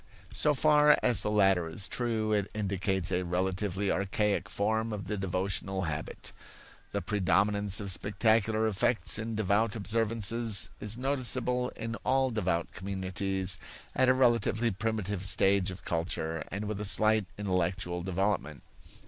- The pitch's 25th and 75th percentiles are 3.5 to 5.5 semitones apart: No, average, 2.9 semitones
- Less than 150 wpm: Yes, average, 140 wpm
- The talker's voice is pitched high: No, low, 100 Hz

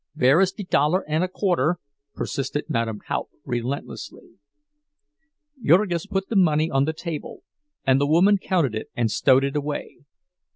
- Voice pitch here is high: No, medium, 150 Hz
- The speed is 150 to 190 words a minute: Yes, average, 155 wpm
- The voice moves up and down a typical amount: Yes, average, 4.9 semitones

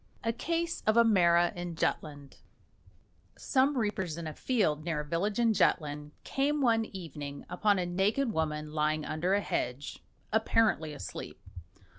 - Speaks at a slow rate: No, average, 150 wpm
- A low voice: No, medium, 175 Hz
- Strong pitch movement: Yes, wide, 6.6 semitones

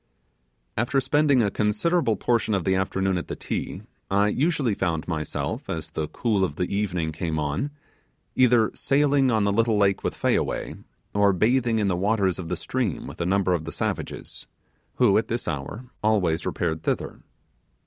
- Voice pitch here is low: Yes, low, 100 Hz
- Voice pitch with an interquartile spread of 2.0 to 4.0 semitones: No, average, 4.9 semitones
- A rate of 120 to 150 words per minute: No, average, 175 wpm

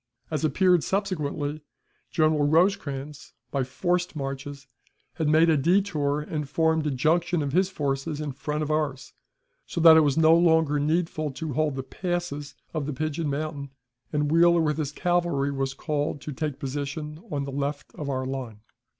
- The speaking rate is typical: Yes, average, 170 wpm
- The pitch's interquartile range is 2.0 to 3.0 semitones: Yes, narrow, 2.4 semitones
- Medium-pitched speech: Yes, medium, 150 Hz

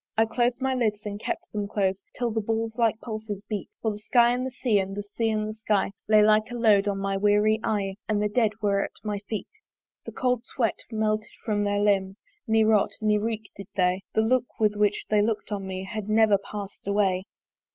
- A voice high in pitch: Yes, high, 215 Hz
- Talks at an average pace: No, fast, 225 wpm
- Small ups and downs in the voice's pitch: Yes, narrow, 1.6 semitones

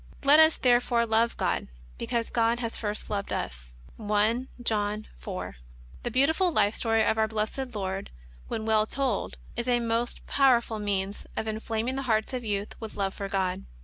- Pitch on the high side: Yes, high, 220 Hz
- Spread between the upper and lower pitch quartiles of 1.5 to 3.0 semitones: Yes, average, 2.7 semitones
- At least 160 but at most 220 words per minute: Yes, average, 175 wpm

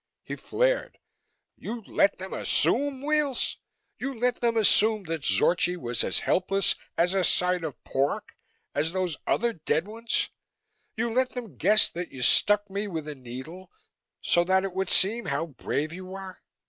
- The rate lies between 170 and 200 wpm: No, average, 160 wpm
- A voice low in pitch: No, high, 190 Hz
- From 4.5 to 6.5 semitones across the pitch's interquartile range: Yes, average, 5.2 semitones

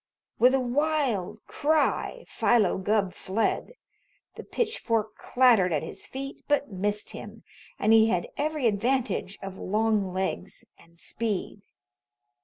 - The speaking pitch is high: Yes, high, 220 Hz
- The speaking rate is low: Yes, slow, 125 wpm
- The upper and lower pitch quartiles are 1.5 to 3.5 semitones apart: No, average, 5.3 semitones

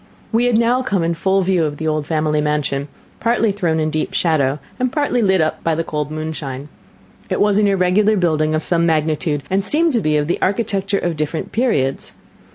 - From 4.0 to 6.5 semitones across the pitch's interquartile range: Yes, average, 4.9 semitones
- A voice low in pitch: No, medium, 165 Hz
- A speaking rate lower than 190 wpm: No, fast, 205 wpm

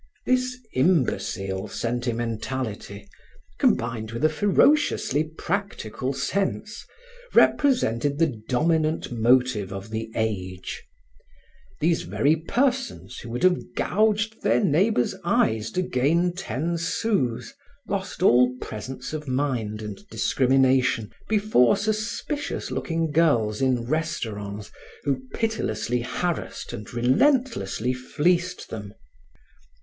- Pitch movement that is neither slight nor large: No, wide, 7.7 semitones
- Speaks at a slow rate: Yes, slow, 100 wpm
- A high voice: No, low, 130 Hz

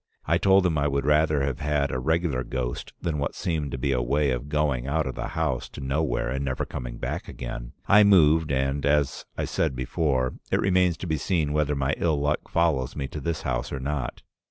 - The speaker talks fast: Yes, fast, 225 wpm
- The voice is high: No, very low, 70 Hz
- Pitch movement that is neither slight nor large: Yes, average, 3.1 semitones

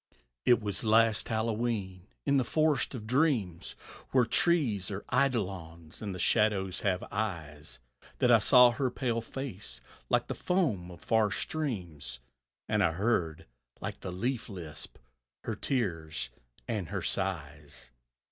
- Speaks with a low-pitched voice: Yes, low, 105 Hz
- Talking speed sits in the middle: No, slow, 130 wpm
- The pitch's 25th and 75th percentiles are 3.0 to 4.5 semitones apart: No, wide, 5.6 semitones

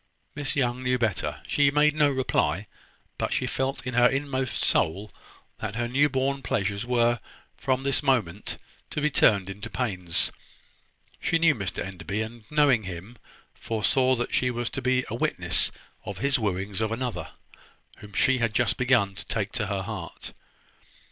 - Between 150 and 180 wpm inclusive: Yes, average, 170 wpm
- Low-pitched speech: Yes, low, 120 Hz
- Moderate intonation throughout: Yes, average, 4.5 semitones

